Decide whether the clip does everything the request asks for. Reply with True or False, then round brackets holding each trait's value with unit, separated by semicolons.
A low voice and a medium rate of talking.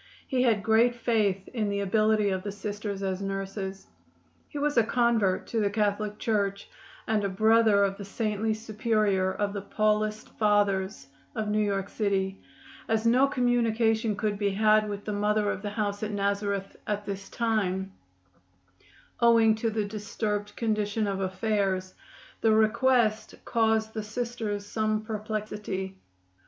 False (210 Hz; 150 wpm)